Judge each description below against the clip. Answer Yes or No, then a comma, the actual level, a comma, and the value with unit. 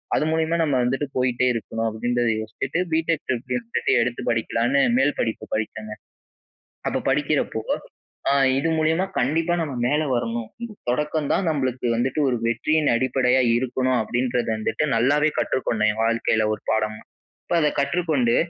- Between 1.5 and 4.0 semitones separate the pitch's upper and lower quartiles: No, average, 4.4 semitones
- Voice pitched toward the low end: Yes, low, 130 Hz